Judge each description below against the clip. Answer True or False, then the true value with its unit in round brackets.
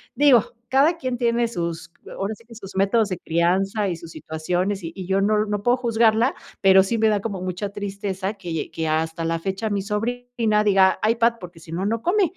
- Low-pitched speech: False (200 Hz)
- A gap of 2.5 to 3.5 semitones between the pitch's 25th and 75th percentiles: False (3.9 semitones)